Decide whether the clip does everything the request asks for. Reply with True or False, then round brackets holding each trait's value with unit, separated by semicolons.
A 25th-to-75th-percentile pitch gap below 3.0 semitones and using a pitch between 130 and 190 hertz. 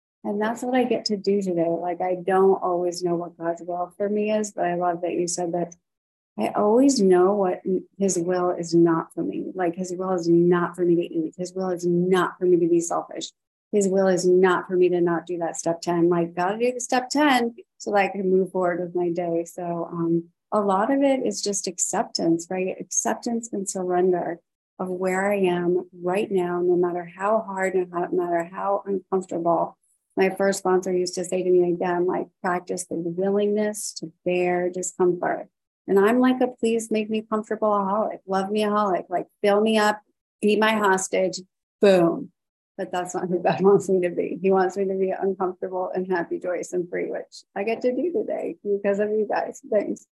True (2.6 semitones; 185 Hz)